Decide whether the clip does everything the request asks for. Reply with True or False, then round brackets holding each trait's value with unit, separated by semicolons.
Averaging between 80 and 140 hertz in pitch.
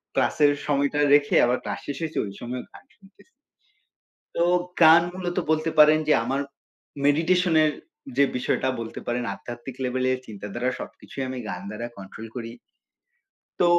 True (135 Hz)